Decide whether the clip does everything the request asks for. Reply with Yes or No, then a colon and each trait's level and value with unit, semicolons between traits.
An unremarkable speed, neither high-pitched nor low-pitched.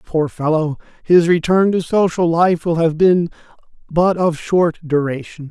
Yes: average, 155 wpm; medium, 165 Hz